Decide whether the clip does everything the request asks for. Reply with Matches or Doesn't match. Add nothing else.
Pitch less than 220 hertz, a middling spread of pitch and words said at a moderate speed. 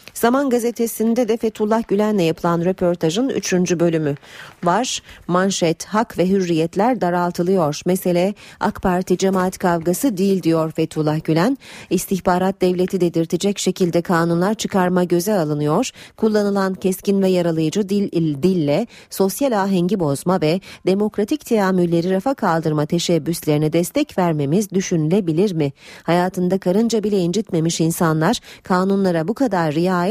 Matches